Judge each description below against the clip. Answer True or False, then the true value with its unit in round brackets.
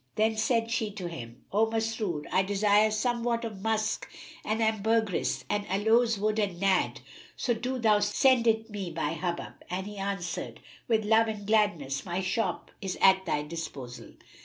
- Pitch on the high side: True (210 Hz)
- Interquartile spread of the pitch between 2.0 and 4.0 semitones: True (3.0 semitones)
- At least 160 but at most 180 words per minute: True (165 wpm)